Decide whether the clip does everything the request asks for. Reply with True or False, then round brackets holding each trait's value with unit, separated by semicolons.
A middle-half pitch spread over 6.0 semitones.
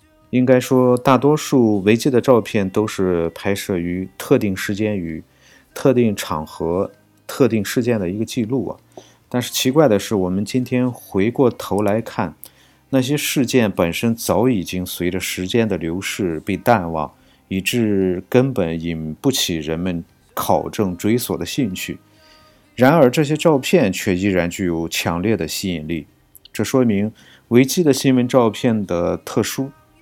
False (5.7 semitones)